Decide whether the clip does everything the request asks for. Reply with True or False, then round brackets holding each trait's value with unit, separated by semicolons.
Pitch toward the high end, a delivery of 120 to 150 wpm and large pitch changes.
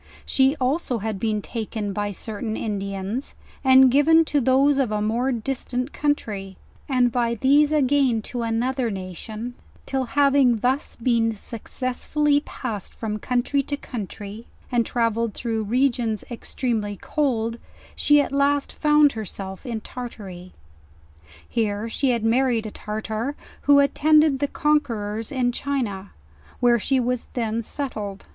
False (240 Hz; 140 wpm; 3.9 semitones)